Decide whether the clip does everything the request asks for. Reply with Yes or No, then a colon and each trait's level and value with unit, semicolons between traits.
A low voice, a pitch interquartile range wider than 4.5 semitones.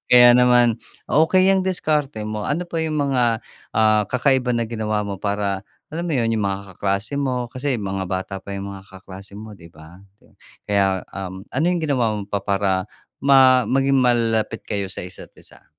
Yes: low, 110 Hz; average, 5.1 semitones